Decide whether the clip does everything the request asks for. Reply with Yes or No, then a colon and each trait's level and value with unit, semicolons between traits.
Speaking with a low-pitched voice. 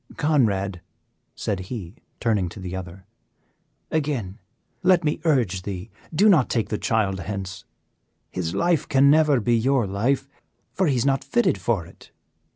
Yes: low, 115 Hz